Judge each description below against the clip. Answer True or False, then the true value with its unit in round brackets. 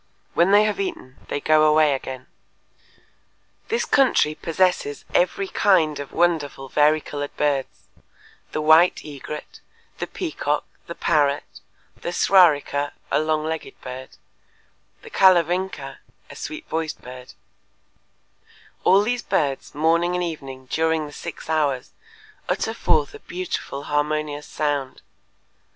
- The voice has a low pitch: False (155 Hz)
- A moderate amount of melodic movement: True (3.5 semitones)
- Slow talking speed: True (120 wpm)